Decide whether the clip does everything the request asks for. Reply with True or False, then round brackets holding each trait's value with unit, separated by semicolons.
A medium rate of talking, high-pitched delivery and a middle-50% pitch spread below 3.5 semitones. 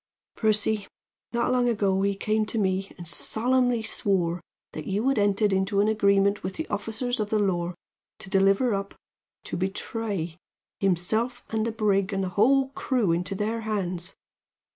True (165 wpm; 205 Hz; 2.6 semitones)